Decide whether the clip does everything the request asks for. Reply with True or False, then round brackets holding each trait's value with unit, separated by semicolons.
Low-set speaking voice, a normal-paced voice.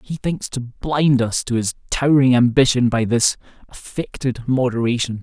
True (125 Hz; 150 wpm)